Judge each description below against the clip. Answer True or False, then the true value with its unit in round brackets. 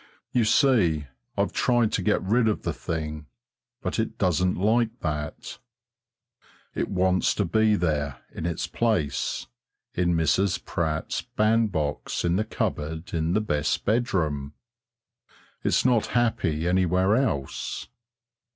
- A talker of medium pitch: False (90 Hz)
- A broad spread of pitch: True (5.7 semitones)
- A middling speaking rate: False (125 wpm)